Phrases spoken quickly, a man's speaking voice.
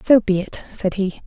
No: fast, 240 wpm; female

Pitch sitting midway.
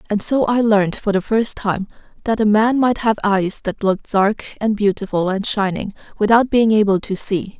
No: high, 210 Hz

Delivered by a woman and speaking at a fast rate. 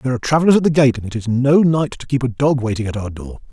No: male; fast, 325 wpm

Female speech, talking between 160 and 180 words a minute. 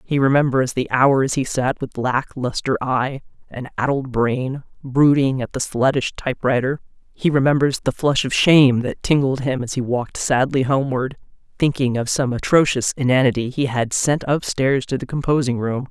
Yes: female; average, 170 wpm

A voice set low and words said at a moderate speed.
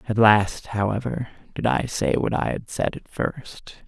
Yes: low, 110 Hz; average, 185 wpm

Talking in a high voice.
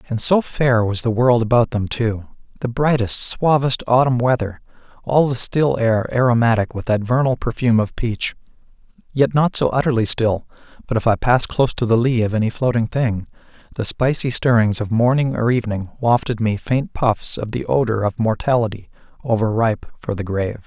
No: low, 120 Hz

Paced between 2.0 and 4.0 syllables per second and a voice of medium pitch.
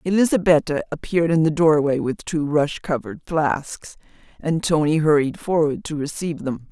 No: 5.2 syllables/s; medium, 155 Hz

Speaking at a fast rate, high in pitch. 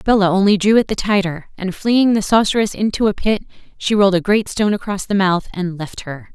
Yes: fast, 225 wpm; high, 200 Hz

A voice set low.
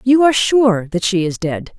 No: high, 210 Hz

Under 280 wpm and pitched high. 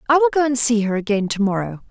No: fast, 285 wpm; high, 235 Hz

